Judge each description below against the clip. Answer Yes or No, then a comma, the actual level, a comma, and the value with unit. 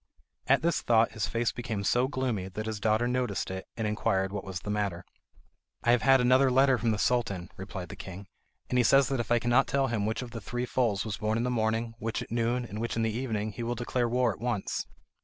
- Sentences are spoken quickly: Yes, fast, 245 wpm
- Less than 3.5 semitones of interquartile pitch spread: Yes, average, 2.8 semitones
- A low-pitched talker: Yes, low, 115 Hz